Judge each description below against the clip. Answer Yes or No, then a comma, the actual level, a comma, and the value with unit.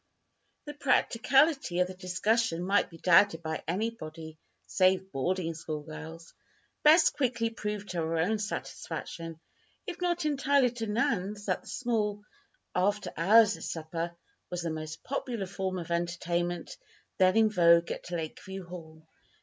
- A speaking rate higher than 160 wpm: No, average, 140 wpm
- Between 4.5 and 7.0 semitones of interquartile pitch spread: Yes, average, 5.0 semitones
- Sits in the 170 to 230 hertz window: Yes, medium, 185 Hz